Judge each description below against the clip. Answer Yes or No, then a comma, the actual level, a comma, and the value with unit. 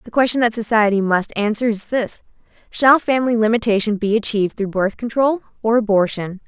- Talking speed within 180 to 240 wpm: No, average, 165 wpm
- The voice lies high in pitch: Yes, high, 220 Hz